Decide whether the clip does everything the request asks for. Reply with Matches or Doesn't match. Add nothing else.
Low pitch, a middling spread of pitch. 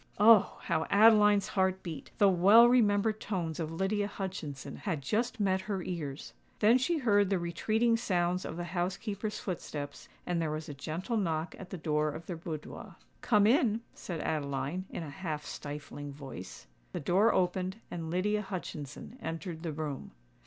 Doesn't match